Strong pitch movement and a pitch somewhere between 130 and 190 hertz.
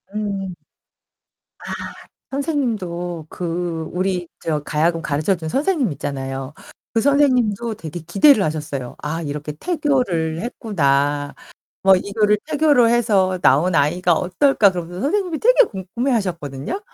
Yes: wide, 7.0 semitones; medium, 185 Hz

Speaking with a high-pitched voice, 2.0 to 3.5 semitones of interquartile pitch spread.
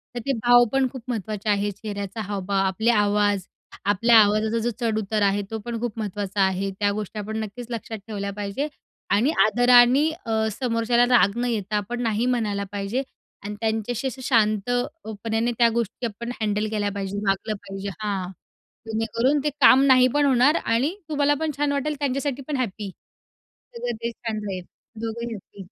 Yes: high, 220 Hz; average, 3.1 semitones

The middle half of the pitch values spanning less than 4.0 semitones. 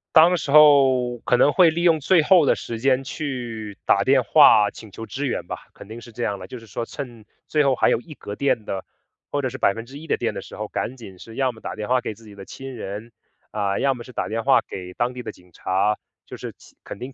No: average, 4.3 semitones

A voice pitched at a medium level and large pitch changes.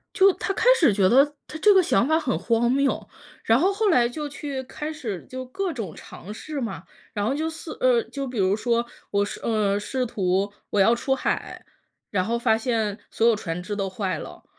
No: high, 235 Hz; wide, 6.2 semitones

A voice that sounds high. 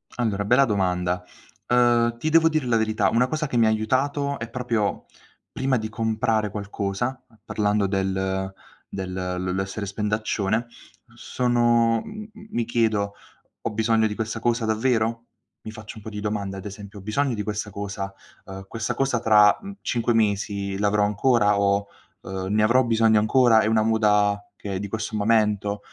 No: low, 110 Hz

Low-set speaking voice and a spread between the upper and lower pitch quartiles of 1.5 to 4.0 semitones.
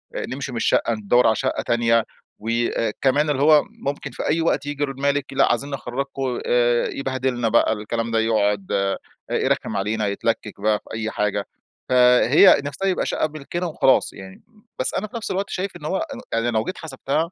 No: low, 125 Hz; average, 4.5 semitones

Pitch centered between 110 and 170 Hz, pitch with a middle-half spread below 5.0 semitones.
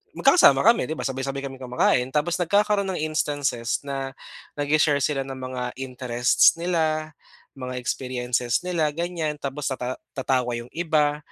Yes: medium, 140 Hz; average, 3.4 semitones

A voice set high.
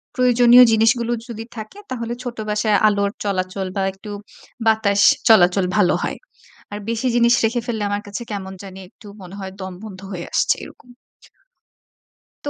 Yes: high, 210 Hz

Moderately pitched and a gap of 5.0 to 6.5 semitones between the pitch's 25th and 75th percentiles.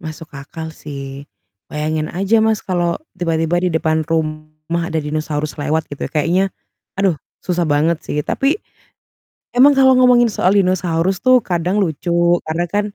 No: medium, 170 Hz; average, 3.6 semitones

